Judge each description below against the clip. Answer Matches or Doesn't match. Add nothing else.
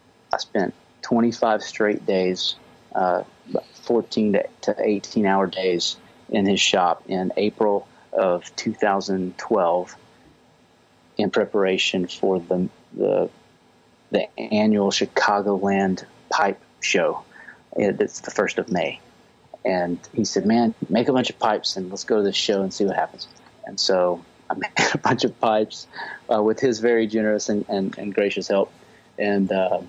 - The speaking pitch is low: Matches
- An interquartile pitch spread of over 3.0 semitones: Doesn't match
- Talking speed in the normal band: Matches